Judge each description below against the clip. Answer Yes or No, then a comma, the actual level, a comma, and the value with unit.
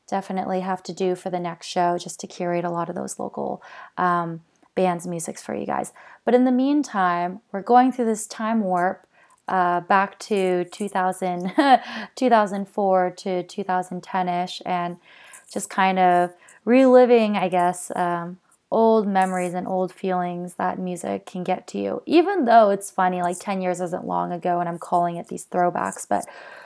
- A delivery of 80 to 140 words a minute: No, average, 170 wpm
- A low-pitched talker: No, medium, 185 Hz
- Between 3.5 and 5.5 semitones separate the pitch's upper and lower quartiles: No, narrow, 2.5 semitones